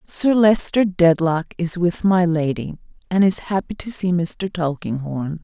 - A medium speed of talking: Yes, average, 155 wpm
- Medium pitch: Yes, medium, 175 Hz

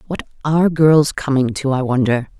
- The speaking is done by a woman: Yes, female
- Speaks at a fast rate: No, average, 175 wpm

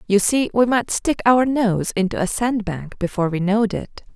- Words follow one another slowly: No, average, 200 wpm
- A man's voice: No, female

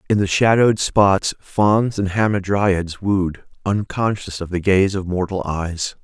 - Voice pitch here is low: Yes, very low, 95 Hz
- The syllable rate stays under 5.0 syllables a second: Yes, 4.0 syllables/s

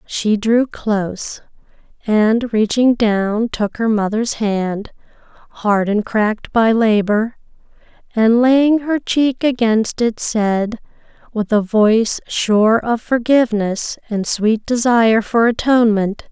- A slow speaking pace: Yes, slow, 120 wpm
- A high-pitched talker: Yes, high, 220 Hz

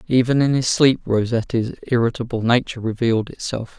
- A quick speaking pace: No, average, 145 wpm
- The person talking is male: Yes, male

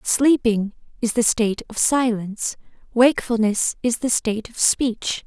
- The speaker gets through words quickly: No, slow, 135 wpm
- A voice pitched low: No, high, 230 Hz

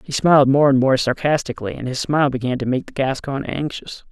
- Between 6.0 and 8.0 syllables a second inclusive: Yes, 6.1 syllables/s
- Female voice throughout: No, male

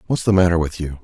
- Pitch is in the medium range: No, very low, 85 Hz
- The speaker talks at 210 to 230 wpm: No, fast, 290 wpm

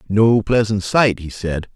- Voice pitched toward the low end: Yes, low, 105 Hz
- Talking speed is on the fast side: No, average, 170 wpm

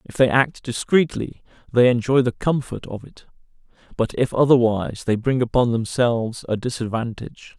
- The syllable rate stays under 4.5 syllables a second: No, 5.1 syllables/s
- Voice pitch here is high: No, low, 120 Hz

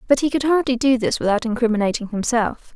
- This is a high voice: Yes, high, 240 Hz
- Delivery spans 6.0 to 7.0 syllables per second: Yes, 6.2 syllables/s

